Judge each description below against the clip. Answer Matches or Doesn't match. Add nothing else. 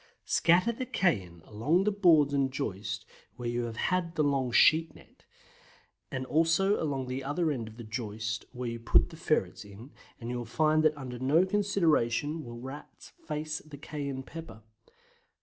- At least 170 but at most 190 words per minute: Matches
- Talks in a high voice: Doesn't match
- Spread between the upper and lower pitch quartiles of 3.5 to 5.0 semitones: Doesn't match